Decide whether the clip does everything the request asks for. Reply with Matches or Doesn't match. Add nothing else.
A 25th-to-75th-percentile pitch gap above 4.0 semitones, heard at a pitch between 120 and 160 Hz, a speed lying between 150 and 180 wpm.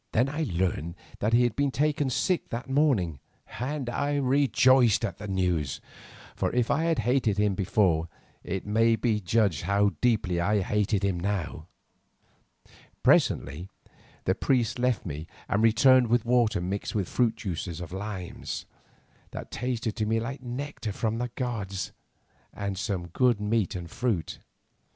Doesn't match